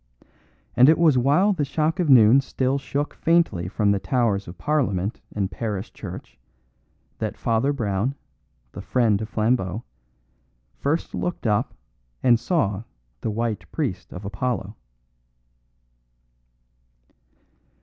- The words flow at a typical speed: No, slow, 120 wpm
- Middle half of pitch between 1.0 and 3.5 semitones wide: No, wide, 5.5 semitones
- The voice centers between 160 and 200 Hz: No, low, 120 Hz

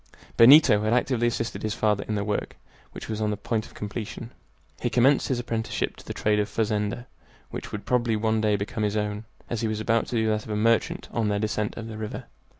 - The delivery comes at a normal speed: No, fast, 240 wpm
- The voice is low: Yes, low, 110 Hz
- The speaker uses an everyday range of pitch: No, narrow, 1.6 semitones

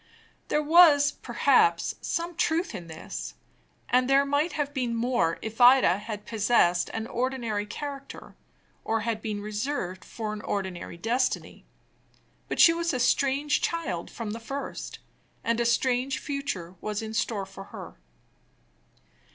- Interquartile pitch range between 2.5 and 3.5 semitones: No, average, 5.0 semitones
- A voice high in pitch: Yes, high, 235 Hz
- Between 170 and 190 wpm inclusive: No, average, 145 wpm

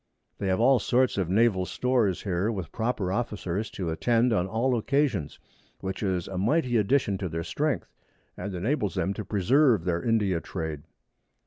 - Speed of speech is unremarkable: Yes, average, 170 wpm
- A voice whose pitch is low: Yes, low, 100 Hz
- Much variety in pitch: No, average, 4.7 semitones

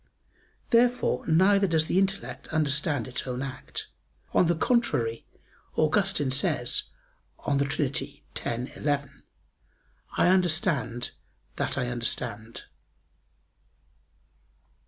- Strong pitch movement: Yes, wide, 6.5 semitones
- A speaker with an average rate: No, slow, 95 wpm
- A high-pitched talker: No, medium, 145 Hz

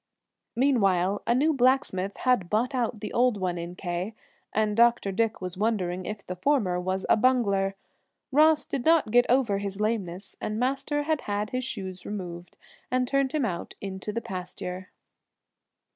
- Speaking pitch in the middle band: No, high, 210 Hz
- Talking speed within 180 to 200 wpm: No, average, 165 wpm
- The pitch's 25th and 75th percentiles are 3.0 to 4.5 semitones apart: No, average, 5.2 semitones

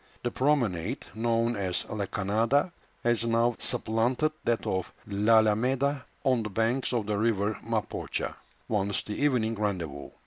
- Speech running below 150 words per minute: Yes, slow, 135 wpm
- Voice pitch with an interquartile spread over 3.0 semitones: No, average, 2.7 semitones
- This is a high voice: No, low, 115 Hz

